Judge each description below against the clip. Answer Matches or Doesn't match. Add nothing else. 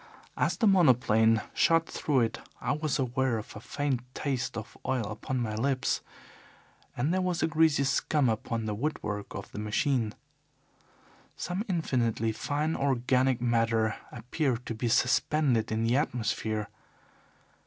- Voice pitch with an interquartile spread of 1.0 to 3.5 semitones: Doesn't match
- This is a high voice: Doesn't match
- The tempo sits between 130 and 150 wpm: Matches